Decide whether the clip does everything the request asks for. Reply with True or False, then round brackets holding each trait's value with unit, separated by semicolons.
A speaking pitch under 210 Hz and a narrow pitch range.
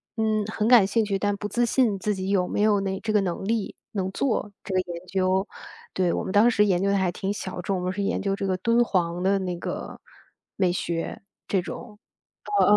True (195 Hz; 2.3 semitones)